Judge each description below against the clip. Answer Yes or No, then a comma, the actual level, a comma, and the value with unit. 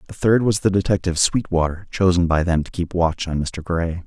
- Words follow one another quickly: Yes, fast, 220 wpm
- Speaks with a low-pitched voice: Yes, very low, 90 Hz